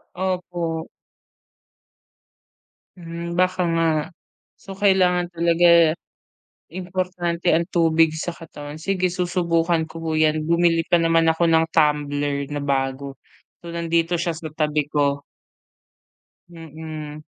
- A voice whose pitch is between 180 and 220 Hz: No, medium, 165 Hz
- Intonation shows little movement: Yes, narrow, 1.9 semitones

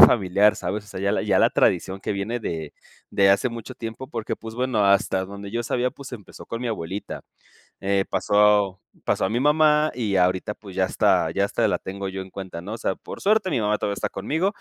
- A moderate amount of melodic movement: Yes, average, 3.5 semitones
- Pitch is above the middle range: No, low, 105 Hz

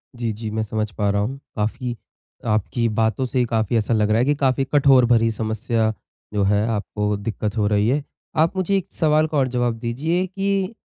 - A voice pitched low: Yes, low, 115 Hz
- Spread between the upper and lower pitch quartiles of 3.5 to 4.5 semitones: Yes, average, 4.2 semitones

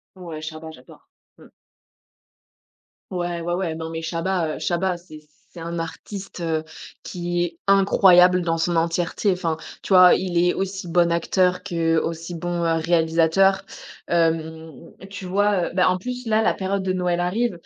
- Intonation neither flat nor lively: No, narrow, 2.1 semitones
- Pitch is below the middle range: No, medium, 175 Hz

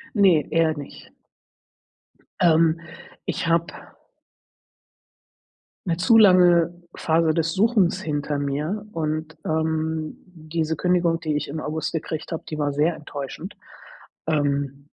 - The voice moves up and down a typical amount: No, narrow, 1.9 semitones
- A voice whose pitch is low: No, medium, 160 Hz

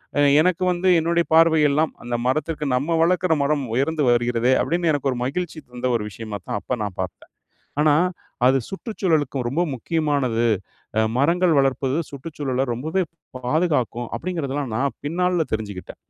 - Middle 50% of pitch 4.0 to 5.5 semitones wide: Yes, average, 4.6 semitones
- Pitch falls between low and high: Yes, medium, 145 Hz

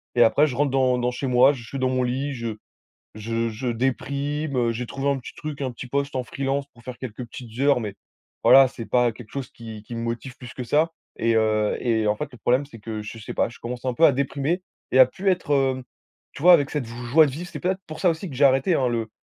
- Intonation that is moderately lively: Yes, average, 3.2 semitones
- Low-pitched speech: Yes, low, 130 Hz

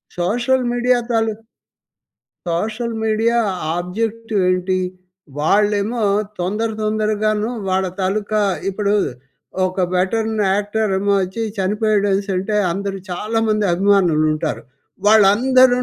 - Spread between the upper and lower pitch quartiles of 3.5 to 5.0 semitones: No, narrow, 2.5 semitones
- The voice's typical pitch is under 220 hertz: Yes, high, 210 Hz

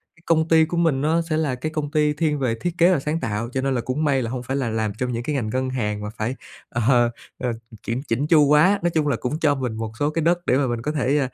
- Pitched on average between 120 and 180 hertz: Yes, medium, 140 Hz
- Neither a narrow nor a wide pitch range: Yes, average, 4.3 semitones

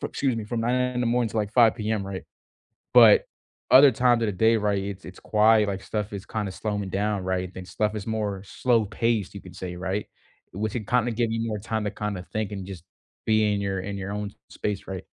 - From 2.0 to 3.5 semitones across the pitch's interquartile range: Yes, narrow, 2.4 semitones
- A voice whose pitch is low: Yes, low, 105 Hz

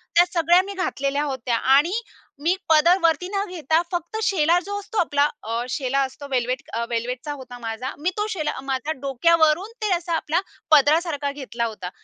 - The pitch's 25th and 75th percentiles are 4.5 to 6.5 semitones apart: Yes, average, 4.9 semitones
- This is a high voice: Yes, very high, 300 Hz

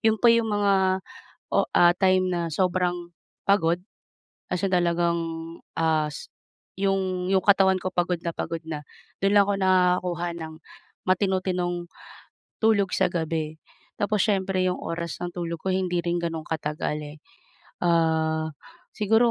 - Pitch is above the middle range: No, medium, 180 Hz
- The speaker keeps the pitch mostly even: Yes, narrow, 2.3 semitones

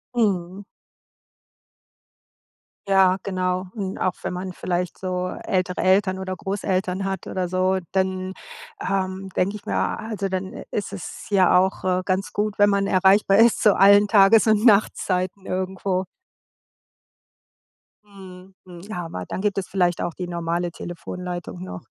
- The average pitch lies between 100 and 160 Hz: No, high, 190 Hz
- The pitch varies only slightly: Yes, narrow, 1.4 semitones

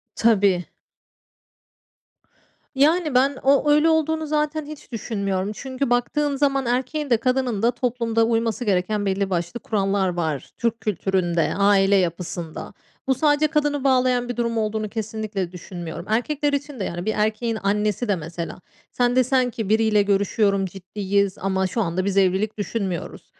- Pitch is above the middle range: Yes, high, 220 Hz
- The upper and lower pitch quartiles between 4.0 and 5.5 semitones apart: Yes, average, 4.9 semitones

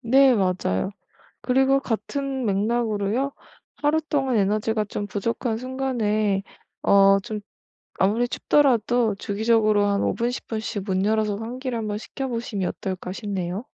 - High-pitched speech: Yes, high, 220 Hz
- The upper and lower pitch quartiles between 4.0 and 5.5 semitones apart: No, average, 3.6 semitones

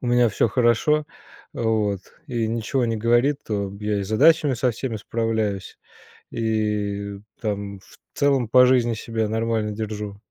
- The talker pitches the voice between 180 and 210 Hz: No, low, 110 Hz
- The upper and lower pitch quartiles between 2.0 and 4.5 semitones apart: Yes, narrow, 2.4 semitones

